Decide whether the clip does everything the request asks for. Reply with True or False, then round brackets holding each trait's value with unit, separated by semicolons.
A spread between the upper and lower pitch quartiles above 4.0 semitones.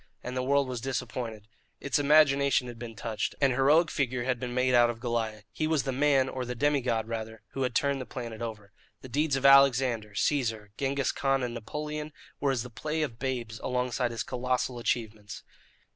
False (3.0 semitones)